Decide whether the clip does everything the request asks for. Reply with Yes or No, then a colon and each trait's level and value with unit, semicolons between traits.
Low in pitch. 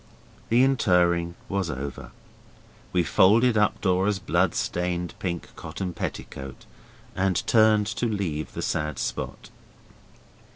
Yes: very low, 90 Hz